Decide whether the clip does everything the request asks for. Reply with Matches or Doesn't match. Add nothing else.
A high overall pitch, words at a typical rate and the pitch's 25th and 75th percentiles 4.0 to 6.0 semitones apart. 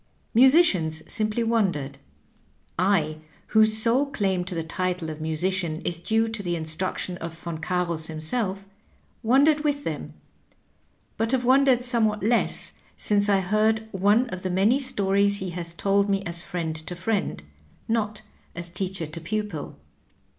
Matches